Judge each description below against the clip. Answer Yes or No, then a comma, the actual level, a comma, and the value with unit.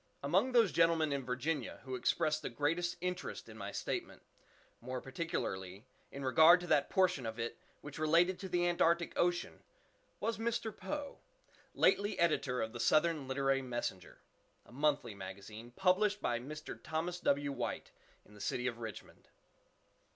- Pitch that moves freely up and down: Yes, wide, 6.1 semitones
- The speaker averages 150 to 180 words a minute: Yes, average, 155 wpm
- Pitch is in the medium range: Yes, medium, 150 Hz